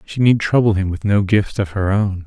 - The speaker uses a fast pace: Yes, fast, 265 wpm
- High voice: No, low, 100 Hz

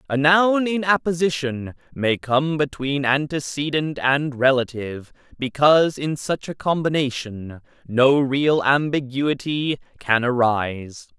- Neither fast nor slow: No, slow, 105 wpm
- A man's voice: Yes, male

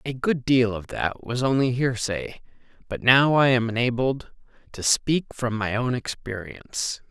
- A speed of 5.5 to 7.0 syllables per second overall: No, 4.3 syllables/s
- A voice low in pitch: Yes, low, 120 Hz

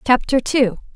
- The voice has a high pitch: Yes, very high, 255 Hz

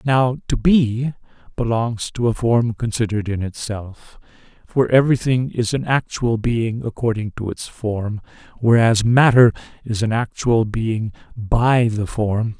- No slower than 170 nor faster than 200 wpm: No, average, 140 wpm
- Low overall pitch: Yes, low, 115 Hz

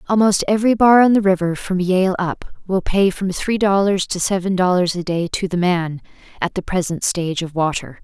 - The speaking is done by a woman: Yes, female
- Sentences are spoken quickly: Yes, fast, 210 wpm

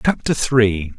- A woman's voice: No, male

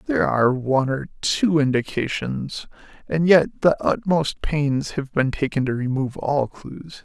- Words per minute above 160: No, average, 155 wpm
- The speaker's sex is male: Yes, male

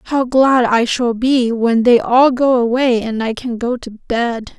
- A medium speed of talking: No, fast, 210 wpm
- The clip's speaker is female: Yes, female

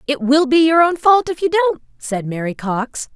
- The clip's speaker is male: No, female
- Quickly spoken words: Yes, fast, 230 wpm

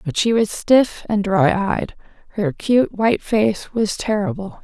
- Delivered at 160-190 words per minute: Yes, average, 170 wpm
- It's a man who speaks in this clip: No, female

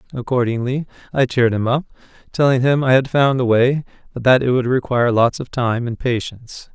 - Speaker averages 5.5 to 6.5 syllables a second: Yes, 5.7 syllables/s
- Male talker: Yes, male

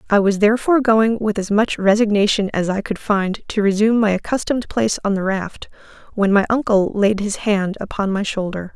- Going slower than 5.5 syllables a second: No, 5.6 syllables/s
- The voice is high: Yes, high, 205 Hz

